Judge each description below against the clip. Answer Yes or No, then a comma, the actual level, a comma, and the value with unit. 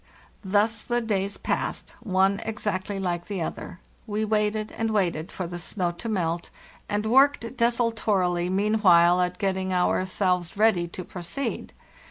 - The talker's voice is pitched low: No, high, 195 Hz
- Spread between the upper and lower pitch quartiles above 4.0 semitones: No, average, 3.4 semitones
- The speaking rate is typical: Yes, average, 150 wpm